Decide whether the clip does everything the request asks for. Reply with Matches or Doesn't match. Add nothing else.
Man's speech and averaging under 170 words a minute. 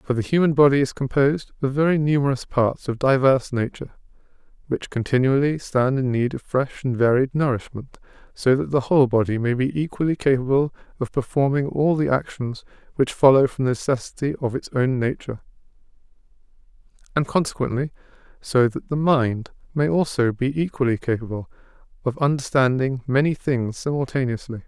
Matches